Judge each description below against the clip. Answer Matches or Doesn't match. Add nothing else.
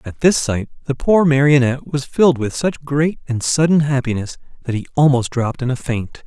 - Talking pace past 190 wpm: Matches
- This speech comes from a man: Matches